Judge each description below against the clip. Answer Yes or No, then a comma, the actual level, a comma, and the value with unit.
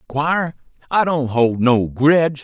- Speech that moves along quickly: No, average, 150 wpm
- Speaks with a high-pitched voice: No, medium, 140 Hz